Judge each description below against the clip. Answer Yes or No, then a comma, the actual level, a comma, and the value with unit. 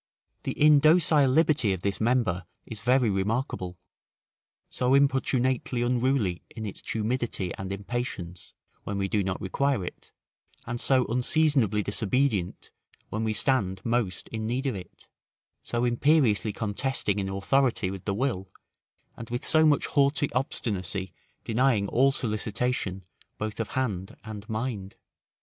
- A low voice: Yes, low, 115 Hz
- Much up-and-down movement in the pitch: No, average, 4.8 semitones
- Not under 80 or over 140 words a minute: Yes, slow, 135 wpm